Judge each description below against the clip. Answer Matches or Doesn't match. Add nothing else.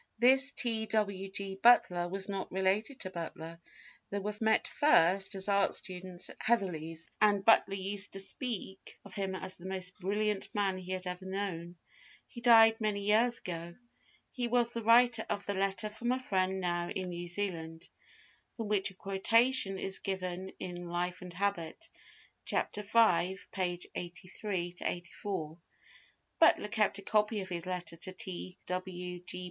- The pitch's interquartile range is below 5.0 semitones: Matches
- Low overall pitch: Doesn't match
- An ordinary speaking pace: Matches